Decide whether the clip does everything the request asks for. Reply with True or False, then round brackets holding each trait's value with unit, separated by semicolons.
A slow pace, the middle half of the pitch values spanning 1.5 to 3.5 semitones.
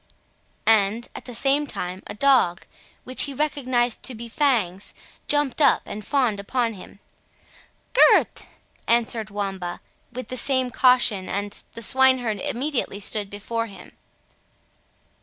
False (130 wpm; 4.3 semitones)